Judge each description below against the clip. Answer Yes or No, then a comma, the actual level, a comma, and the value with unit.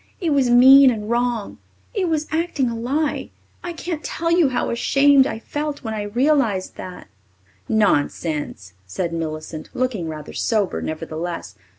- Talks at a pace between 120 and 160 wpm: Yes, average, 150 wpm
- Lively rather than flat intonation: Yes, wide, 8.0 semitones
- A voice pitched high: Yes, high, 240 Hz